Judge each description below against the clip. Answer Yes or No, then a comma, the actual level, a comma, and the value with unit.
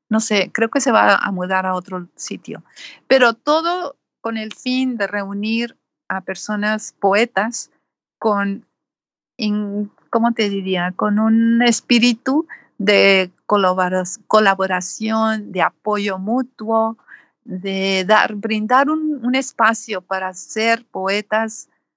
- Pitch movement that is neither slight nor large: Yes, average, 3.1 semitones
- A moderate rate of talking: No, slow, 115 wpm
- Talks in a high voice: Yes, high, 215 Hz